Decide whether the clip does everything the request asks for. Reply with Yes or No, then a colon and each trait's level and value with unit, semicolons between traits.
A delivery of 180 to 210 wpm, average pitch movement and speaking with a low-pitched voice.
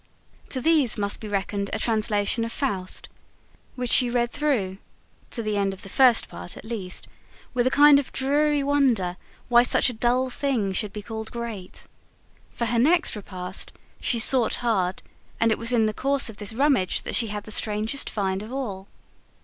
No: average, 190 wpm; average, 4.1 semitones; high, 230 Hz